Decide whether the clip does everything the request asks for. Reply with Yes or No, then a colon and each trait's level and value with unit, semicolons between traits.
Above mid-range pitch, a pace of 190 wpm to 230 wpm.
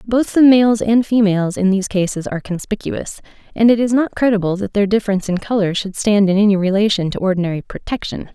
Yes: high, 205 Hz; average, 200 wpm